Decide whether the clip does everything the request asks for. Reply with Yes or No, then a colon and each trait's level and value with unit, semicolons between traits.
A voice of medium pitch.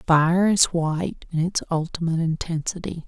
Yes: medium, 170 Hz